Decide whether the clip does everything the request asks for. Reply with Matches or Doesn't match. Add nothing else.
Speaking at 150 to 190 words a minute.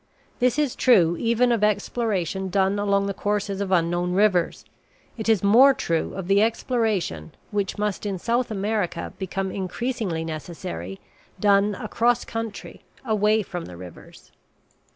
Doesn't match